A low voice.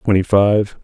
Yes: low, 100 Hz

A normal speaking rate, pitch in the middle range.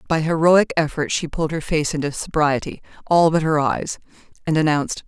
Yes: average, 155 wpm; medium, 155 Hz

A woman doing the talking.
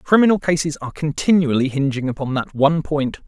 No: male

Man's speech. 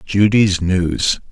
Yes: male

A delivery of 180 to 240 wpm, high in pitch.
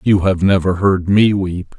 No: average, 200 wpm; very low, 95 Hz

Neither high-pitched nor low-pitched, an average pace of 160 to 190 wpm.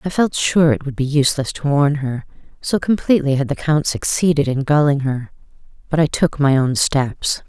No: medium, 145 Hz; average, 200 wpm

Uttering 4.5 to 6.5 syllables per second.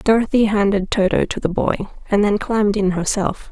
Yes: 5.4 syllables/s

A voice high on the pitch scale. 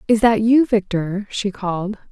Yes: high, 205 Hz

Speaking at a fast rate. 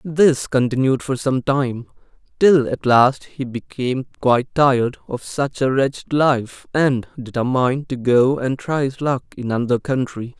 No: average, 160 wpm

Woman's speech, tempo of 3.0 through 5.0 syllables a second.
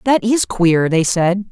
Yes: female; 3.6 syllables/s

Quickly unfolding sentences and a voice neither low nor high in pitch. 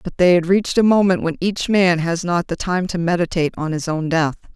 Yes: fast, 250 wpm; medium, 175 Hz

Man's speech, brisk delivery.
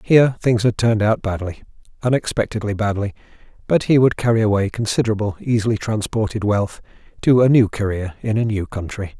No: male; average, 155 wpm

